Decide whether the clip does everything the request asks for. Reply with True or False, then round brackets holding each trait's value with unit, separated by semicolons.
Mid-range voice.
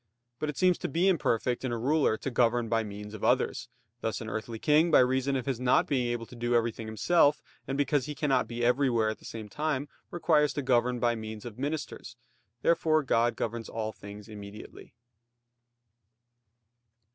False (120 Hz)